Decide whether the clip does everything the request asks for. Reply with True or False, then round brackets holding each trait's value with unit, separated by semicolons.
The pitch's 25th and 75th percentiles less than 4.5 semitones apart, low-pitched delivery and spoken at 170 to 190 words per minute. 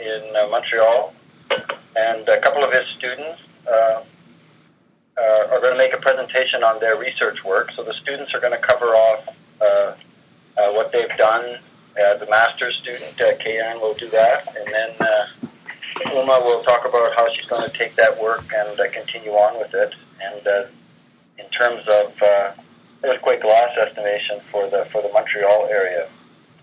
True (3.2 semitones; 110 Hz; 175 wpm)